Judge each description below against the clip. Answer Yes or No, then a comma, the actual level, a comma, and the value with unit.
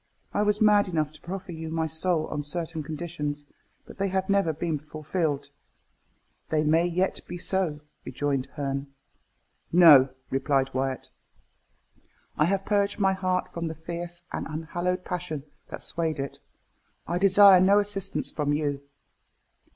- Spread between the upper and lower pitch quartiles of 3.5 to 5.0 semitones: Yes, average, 3.8 semitones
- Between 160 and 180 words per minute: No, average, 145 wpm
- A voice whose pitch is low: No, medium, 165 Hz